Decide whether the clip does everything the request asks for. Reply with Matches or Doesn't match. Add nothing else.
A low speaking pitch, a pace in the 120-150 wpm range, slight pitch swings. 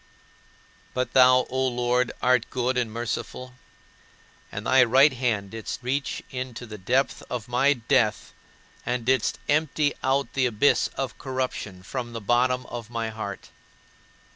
Matches